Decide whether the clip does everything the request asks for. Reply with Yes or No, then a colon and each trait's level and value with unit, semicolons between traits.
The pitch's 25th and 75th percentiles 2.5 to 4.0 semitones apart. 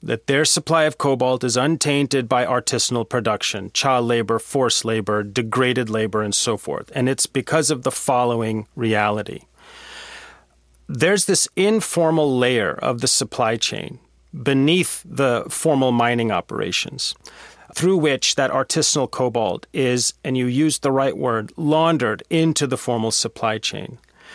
No: average, 4.6 semitones